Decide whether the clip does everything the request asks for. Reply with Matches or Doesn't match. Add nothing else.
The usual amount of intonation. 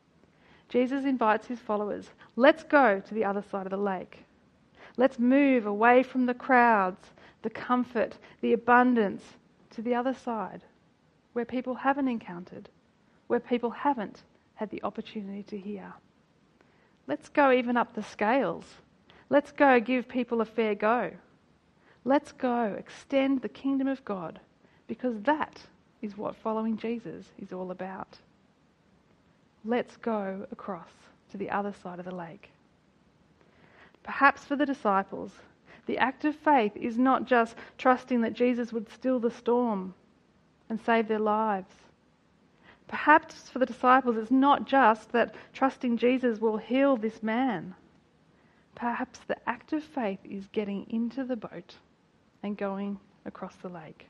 Matches